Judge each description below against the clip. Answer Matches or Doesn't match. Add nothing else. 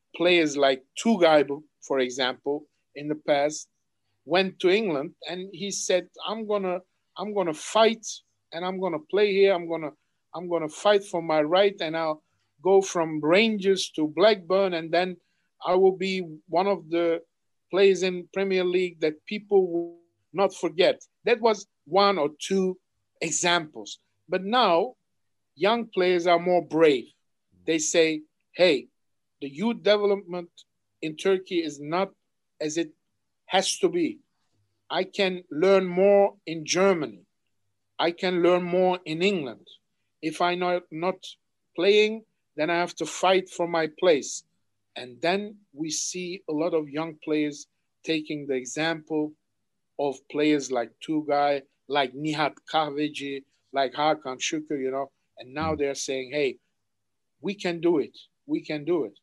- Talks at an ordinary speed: Matches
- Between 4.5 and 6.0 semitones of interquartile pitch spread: Doesn't match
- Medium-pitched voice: Matches